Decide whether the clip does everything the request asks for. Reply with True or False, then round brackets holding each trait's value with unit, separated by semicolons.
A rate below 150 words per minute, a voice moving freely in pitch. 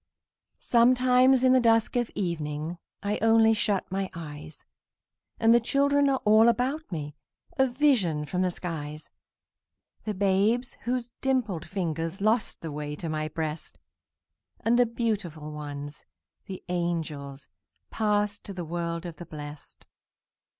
True (135 wpm; 6.8 semitones)